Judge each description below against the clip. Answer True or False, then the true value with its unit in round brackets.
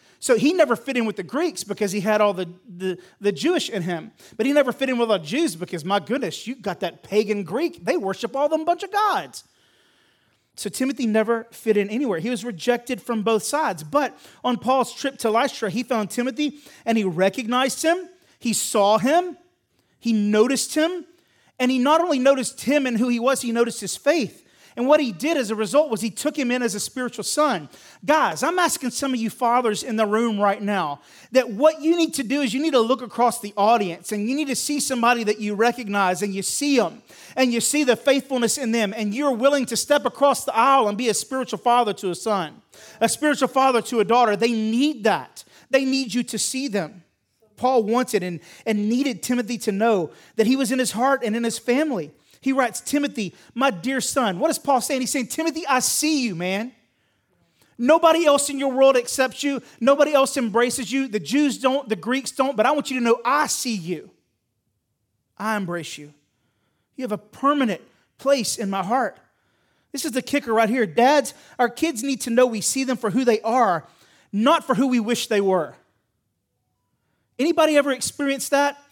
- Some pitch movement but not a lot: True (4.4 semitones)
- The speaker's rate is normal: False (215 wpm)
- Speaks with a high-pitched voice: True (245 Hz)